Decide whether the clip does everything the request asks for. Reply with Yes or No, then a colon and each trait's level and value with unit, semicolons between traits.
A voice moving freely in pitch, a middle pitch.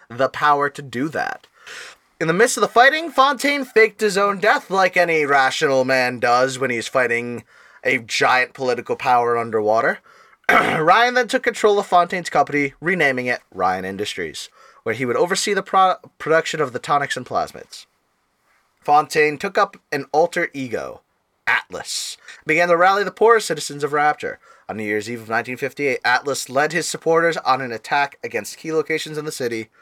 Yes: wide, 6.9 semitones; medium, 150 Hz